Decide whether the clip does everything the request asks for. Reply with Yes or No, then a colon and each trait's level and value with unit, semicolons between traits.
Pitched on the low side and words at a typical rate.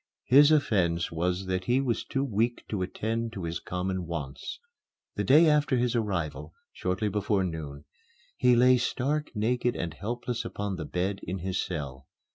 Yes: low, 100 Hz; average, 165 wpm